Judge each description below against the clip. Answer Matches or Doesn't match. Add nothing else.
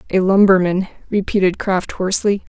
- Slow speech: Matches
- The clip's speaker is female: Matches